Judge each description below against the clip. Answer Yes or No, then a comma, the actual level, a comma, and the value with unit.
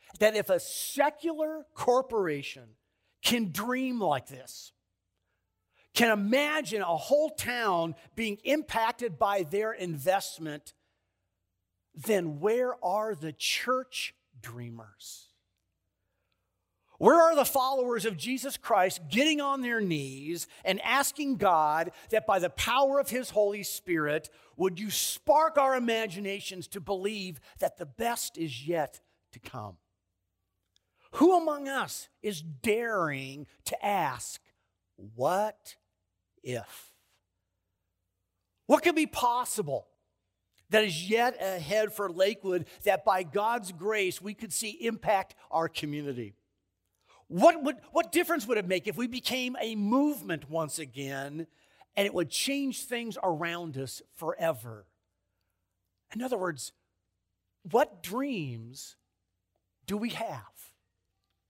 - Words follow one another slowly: Yes, slow, 115 wpm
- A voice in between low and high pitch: Yes, medium, 180 Hz